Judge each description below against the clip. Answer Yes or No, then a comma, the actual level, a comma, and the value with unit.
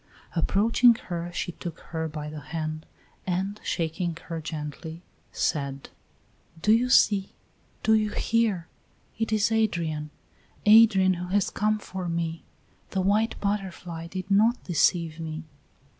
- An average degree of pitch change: Yes, average, 4.3 semitones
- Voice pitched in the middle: Yes, medium, 180 Hz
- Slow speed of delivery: Yes, slow, 130 wpm